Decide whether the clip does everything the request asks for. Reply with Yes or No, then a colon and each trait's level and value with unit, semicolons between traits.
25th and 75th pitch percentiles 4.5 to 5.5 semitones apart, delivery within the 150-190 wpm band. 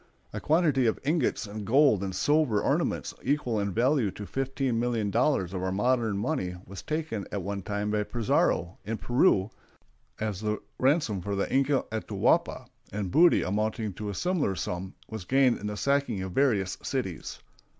Yes: average, 5.2 semitones; average, 170 wpm